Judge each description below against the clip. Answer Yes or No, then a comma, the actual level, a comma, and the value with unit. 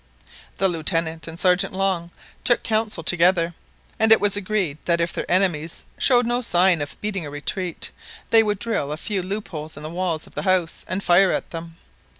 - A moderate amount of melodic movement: Yes, average, 3.7 semitones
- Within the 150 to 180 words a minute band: No, average, 190 wpm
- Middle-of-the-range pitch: Yes, medium, 180 Hz